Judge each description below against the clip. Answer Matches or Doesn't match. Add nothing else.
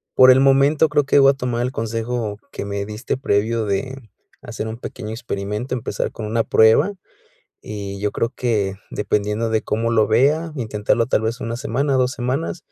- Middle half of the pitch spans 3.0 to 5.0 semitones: Matches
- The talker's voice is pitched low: Matches